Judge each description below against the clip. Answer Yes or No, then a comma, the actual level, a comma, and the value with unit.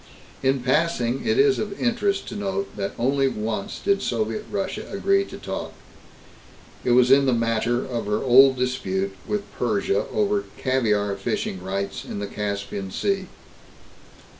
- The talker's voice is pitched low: Yes, low, 125 Hz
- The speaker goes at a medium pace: Yes, average, 150 wpm